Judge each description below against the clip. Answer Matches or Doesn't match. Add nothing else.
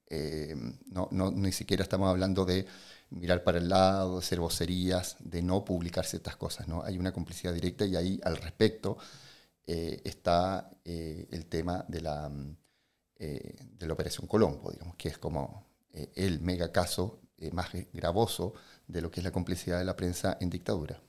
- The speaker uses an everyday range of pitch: Doesn't match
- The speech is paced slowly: Doesn't match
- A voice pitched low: Matches